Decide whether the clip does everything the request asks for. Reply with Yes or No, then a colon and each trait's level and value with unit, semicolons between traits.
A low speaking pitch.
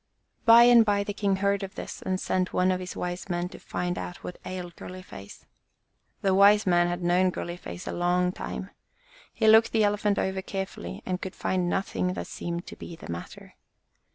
No: medium, 185 Hz